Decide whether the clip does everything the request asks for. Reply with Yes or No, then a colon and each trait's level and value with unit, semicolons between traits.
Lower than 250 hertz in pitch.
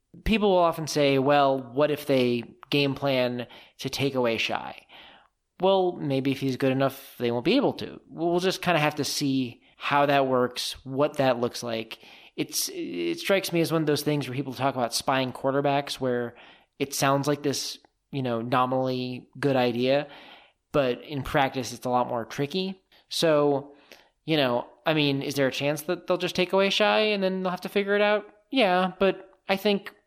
Yes: medium, 140 Hz